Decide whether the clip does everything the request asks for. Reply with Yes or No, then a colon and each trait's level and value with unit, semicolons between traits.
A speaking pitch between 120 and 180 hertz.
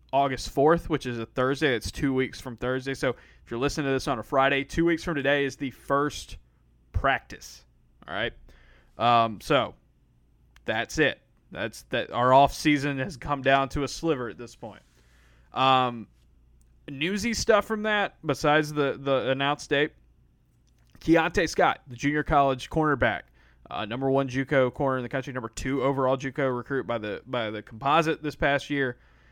Yes: low, 135 Hz